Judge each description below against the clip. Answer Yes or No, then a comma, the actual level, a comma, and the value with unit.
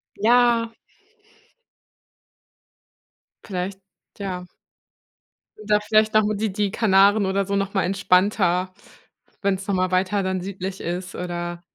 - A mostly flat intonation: Yes, narrow, 2.2 semitones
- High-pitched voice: Yes, high, 195 Hz